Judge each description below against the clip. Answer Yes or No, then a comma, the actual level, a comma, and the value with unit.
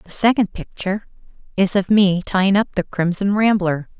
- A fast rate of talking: No, average, 165 wpm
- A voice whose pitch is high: Yes, high, 195 Hz